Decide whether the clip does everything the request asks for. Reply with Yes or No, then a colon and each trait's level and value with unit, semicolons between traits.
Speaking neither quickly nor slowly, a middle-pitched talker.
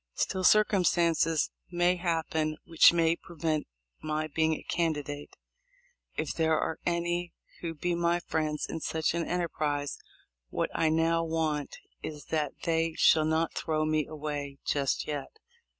Yes: average, 145 wpm; medium, 160 Hz